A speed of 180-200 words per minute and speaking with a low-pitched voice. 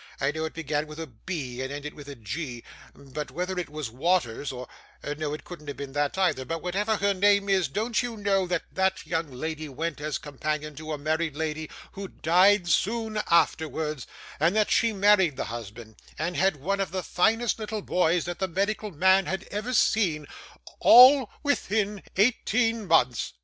No: average, 185 wpm; medium, 170 Hz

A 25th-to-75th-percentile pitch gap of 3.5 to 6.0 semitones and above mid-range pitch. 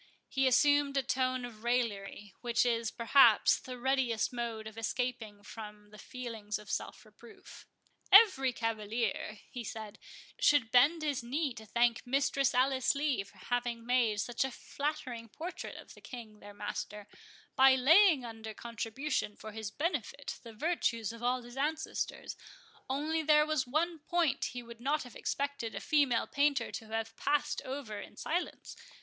Yes: average, 3.9 semitones; high, 245 Hz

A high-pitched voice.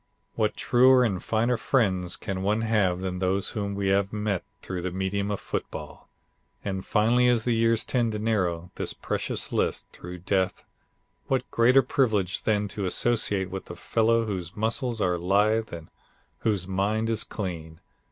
No: low, 100 Hz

